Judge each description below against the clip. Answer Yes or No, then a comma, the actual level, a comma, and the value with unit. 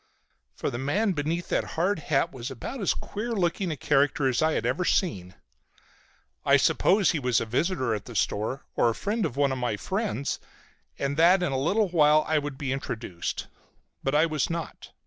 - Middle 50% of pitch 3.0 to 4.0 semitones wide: No, average, 5.1 semitones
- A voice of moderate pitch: Yes, medium, 150 Hz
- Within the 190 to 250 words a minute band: Yes, average, 200 wpm